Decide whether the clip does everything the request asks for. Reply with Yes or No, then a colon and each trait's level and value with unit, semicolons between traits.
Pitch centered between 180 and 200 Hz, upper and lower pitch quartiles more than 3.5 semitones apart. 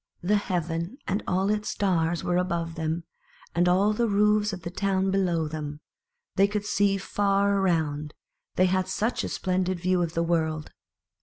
No: medium, 185 Hz; average, 3.1 semitones